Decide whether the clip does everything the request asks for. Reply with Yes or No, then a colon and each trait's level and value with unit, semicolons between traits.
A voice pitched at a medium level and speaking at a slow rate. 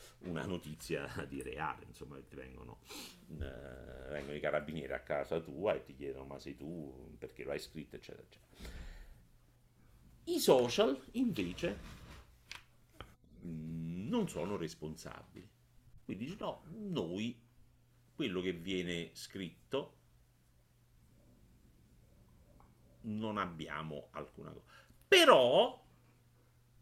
No: very low, 85 Hz; slow, 100 wpm